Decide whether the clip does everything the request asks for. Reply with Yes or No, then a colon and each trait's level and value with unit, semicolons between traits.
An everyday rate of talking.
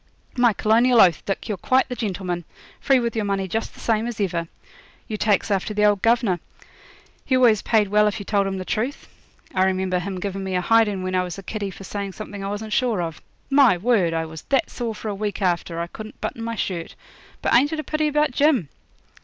No: fast, 230 wpm